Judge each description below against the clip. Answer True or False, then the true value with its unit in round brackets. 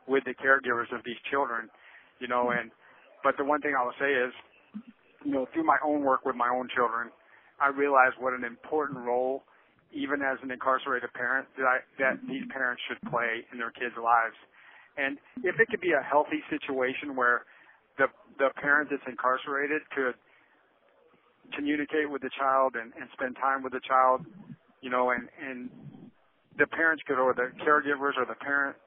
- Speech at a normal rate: True (180 wpm)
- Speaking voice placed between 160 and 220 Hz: False (135 Hz)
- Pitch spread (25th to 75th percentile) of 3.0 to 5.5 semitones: False (2.6 semitones)